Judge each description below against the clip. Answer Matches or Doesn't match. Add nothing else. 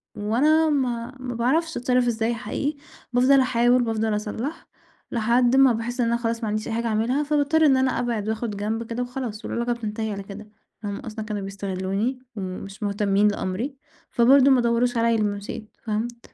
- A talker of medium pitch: Doesn't match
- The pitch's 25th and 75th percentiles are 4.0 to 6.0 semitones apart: Doesn't match